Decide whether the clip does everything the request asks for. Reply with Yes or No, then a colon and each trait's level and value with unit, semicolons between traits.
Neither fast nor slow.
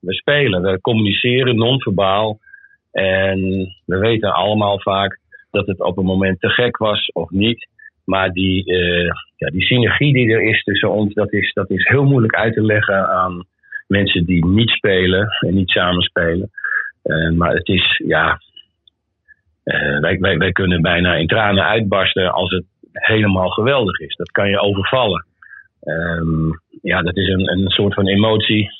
Yes: average, 170 wpm